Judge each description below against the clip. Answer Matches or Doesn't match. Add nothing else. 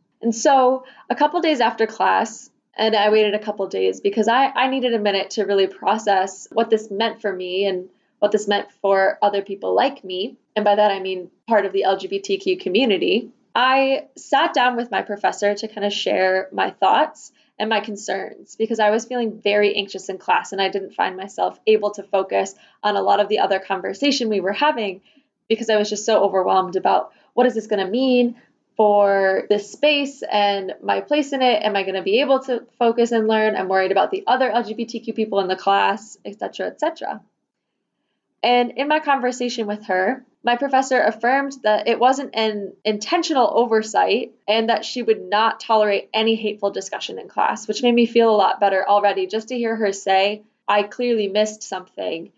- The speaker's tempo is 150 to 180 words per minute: Doesn't match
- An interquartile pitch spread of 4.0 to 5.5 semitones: Doesn't match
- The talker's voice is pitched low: Doesn't match